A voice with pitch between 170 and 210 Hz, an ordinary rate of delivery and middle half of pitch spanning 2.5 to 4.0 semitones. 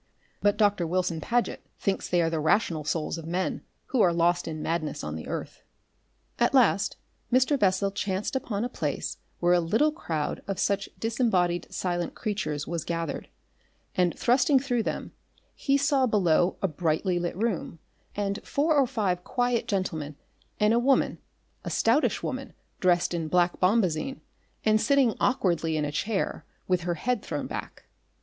No: medium, 185 Hz; average, 165 wpm; average, 5.3 semitones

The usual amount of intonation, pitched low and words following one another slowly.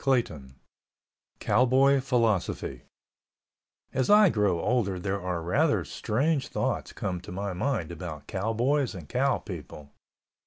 No: wide, 6.6 semitones; low, 105 Hz; slow, 125 wpm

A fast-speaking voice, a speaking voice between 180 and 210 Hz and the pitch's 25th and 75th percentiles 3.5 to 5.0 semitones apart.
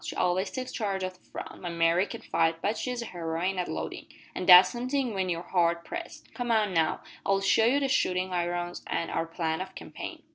Yes: fast, 215 wpm; medium, 185 Hz; average, 4.4 semitones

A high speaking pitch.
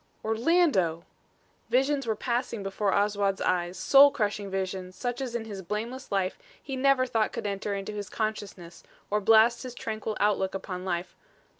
Yes: high, 210 Hz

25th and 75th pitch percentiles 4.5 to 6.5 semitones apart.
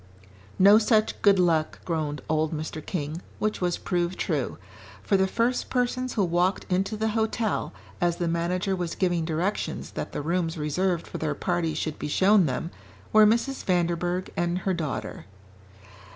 No: average, 3.6 semitones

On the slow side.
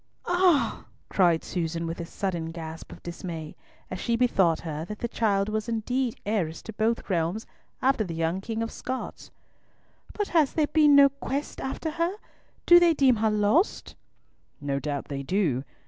No: average, 170 wpm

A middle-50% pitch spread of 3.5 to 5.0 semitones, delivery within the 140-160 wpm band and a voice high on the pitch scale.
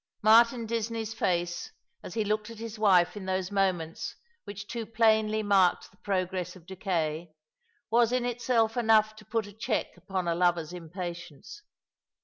Yes: average, 3.8 semitones; average, 155 wpm; high, 205 Hz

